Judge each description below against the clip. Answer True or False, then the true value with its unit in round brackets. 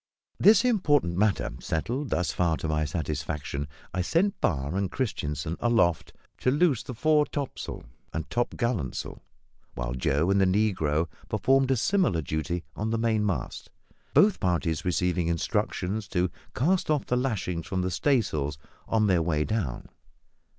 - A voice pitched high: False (95 Hz)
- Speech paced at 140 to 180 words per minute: True (145 wpm)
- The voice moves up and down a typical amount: False (7.6 semitones)